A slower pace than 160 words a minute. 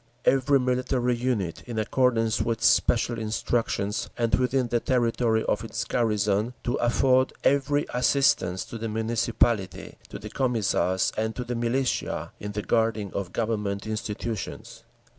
Yes: average, 140 wpm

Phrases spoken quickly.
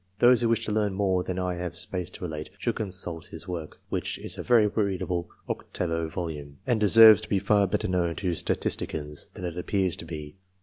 Yes: fast, 215 wpm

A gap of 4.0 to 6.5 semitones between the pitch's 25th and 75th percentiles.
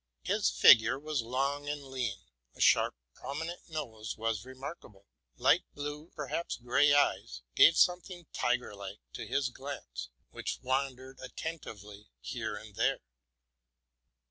Yes: average, 5.0 semitones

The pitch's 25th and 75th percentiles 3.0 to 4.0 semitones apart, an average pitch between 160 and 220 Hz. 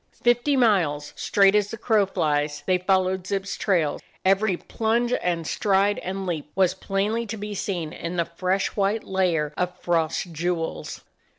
Yes: average, 3.3 semitones; high, 190 Hz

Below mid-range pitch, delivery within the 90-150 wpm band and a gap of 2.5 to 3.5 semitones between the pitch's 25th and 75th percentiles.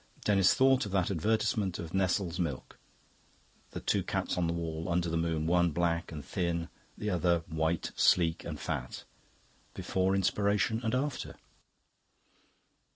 Yes: very low, 85 Hz; average, 145 wpm; average, 2.8 semitones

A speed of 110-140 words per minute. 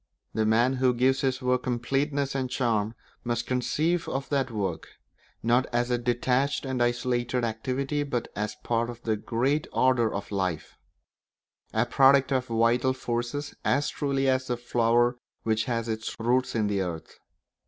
No: average, 165 wpm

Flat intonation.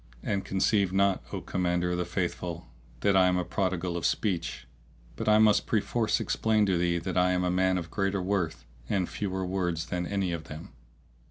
Yes: narrow, 2.0 semitones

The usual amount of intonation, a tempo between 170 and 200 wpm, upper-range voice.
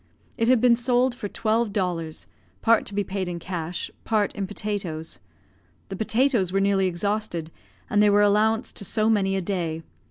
Yes: average, 3.2 semitones; average, 180 wpm; high, 205 Hz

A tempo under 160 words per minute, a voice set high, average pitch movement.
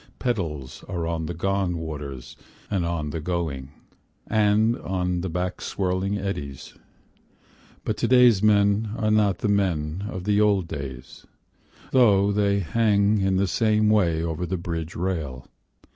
No: average, 145 wpm; very low, 95 Hz; average, 4.0 semitones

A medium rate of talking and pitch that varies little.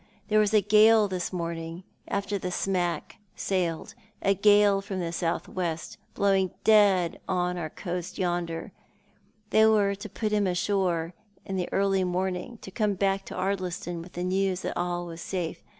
Yes: average, 180 wpm; narrow, 2.2 semitones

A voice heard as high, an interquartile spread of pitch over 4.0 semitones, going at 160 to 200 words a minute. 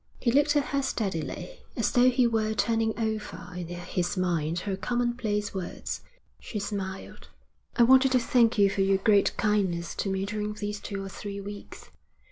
No: high, 205 Hz; average, 3.3 semitones; average, 175 wpm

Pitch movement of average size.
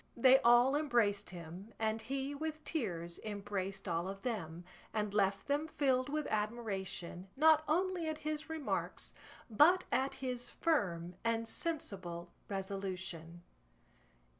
No: wide, 6.9 semitones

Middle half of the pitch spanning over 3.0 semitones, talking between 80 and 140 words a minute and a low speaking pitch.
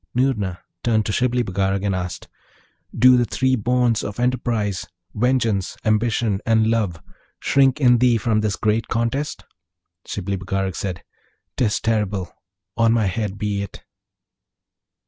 Yes: average, 3.5 semitones; slow, 135 wpm; low, 110 Hz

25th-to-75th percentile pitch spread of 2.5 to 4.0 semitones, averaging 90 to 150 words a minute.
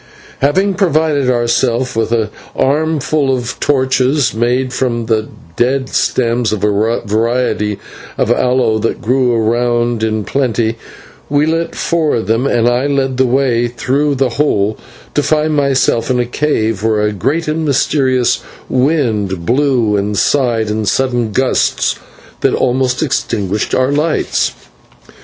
Yes: average, 3.5 semitones; average, 140 wpm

